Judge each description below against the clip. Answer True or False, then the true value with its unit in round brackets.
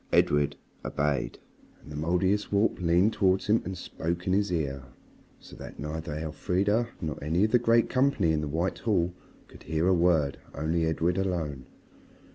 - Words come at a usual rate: True (165 wpm)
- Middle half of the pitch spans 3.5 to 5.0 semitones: True (3.9 semitones)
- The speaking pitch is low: True (85 Hz)